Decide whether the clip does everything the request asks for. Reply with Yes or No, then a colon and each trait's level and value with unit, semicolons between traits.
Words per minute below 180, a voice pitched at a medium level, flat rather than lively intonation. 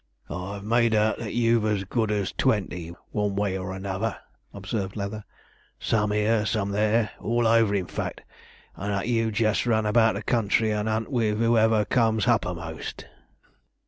No: average, 160 wpm; low, 105 Hz; narrow, 2.1 semitones